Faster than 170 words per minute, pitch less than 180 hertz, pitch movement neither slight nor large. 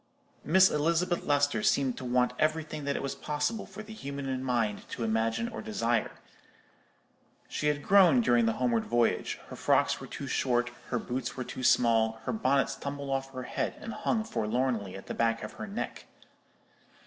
Yes: average, 180 wpm; low, 135 Hz; average, 4.4 semitones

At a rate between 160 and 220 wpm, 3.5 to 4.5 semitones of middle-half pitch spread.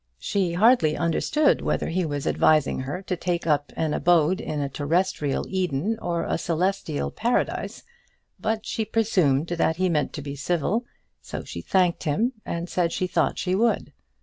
Yes: average, 170 wpm; average, 4.1 semitones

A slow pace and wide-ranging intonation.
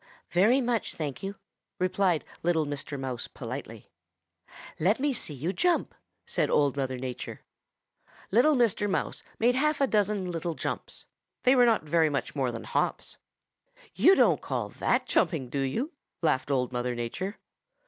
No: average, 150 wpm; wide, 8.9 semitones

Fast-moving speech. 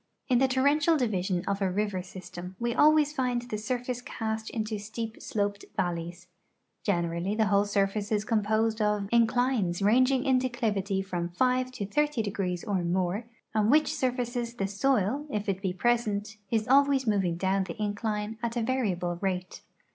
No: average, 165 wpm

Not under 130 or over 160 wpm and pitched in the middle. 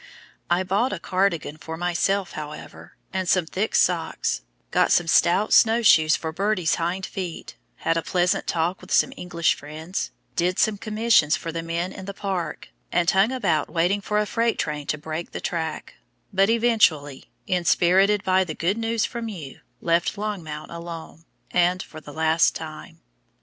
No: average, 170 wpm; medium, 175 Hz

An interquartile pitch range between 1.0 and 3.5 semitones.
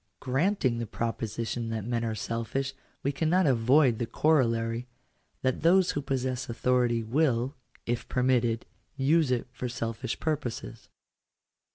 Yes: average, 3.0 semitones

